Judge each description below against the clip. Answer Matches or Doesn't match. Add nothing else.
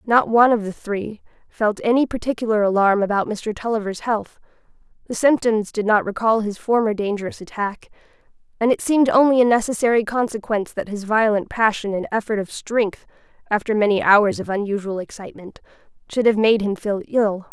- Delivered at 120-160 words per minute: Doesn't match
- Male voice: Doesn't match